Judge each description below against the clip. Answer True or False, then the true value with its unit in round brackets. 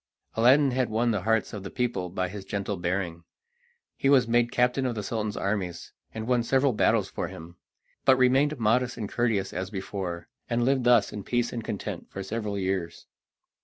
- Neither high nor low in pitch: False (110 Hz)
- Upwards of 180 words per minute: True (190 wpm)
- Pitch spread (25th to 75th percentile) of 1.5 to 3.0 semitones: False (4.1 semitones)